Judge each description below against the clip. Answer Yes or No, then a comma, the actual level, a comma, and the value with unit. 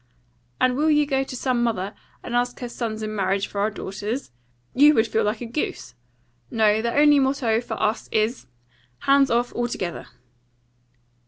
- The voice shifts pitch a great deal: No, average, 3.7 semitones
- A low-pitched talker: No, high, 235 Hz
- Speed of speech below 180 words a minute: Yes, average, 170 wpm